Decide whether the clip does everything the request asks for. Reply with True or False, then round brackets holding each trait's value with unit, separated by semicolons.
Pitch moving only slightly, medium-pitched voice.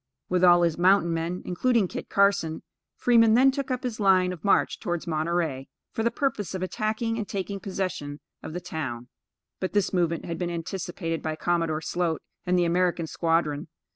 False (3.3 semitones; 180 Hz)